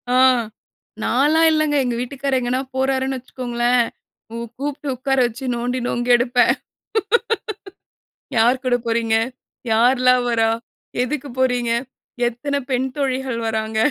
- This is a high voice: Yes, very high, 250 Hz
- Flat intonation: Yes, narrow, 1.9 semitones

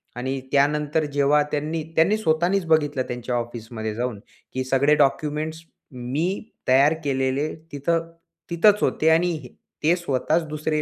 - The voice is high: No, medium, 150 Hz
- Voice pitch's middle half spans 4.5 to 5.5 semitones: No, average, 3.5 semitones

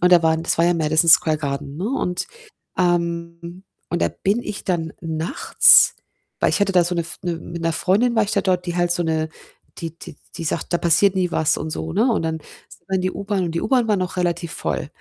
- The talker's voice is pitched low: No, medium, 175 Hz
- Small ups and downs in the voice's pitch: Yes, narrow, 2.3 semitones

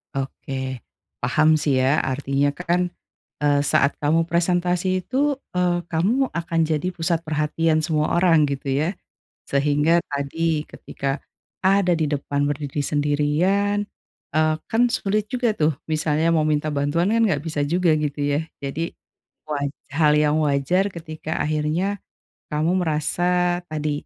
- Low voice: No, medium, 155 Hz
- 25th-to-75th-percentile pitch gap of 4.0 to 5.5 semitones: No, average, 3.2 semitones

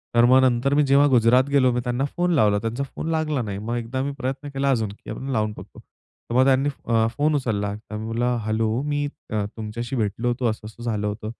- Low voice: Yes, low, 120 Hz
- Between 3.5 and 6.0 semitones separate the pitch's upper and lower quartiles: Yes, average, 3.8 semitones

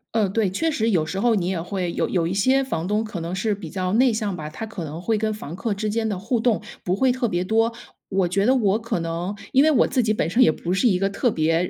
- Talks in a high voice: Yes, high, 205 Hz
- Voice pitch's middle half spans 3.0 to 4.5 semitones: Yes, average, 4.0 semitones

